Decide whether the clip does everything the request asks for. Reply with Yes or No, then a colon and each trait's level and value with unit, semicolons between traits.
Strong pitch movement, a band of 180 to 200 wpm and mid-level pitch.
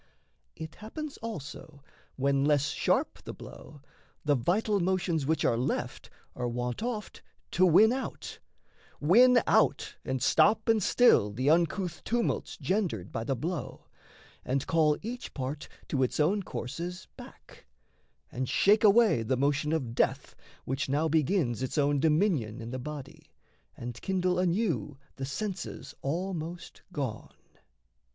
No: wide, 6.3 semitones; average, 140 wpm; medium, 155 Hz